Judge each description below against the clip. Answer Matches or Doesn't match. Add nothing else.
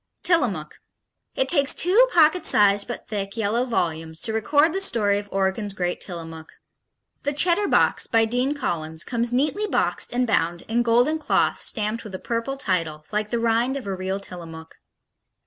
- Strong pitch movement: Matches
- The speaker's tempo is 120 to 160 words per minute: Doesn't match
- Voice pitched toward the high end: Matches